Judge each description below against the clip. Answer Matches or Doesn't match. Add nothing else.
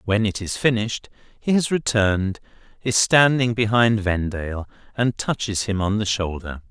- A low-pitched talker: Matches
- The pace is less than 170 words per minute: Matches